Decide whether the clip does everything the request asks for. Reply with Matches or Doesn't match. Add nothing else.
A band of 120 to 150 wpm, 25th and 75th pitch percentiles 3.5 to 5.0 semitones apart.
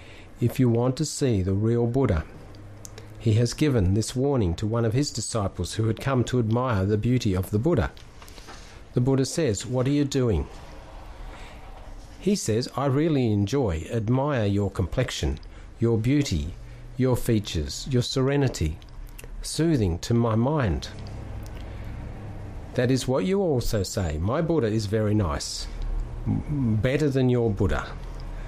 Matches